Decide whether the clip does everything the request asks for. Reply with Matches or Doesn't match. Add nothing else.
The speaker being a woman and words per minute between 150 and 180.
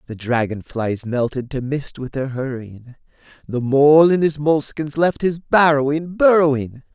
Doesn't match